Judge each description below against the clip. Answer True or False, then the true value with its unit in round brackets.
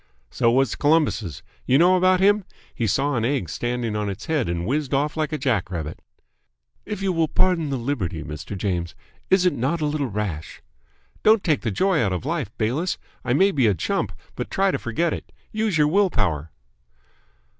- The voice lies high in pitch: False (135 Hz)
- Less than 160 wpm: False (200 wpm)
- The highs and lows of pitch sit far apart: True (8.4 semitones)